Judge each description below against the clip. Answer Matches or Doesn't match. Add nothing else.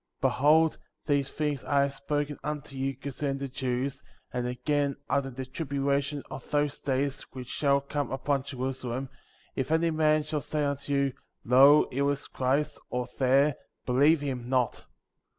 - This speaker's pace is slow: Doesn't match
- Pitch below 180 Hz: Matches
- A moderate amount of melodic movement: Doesn't match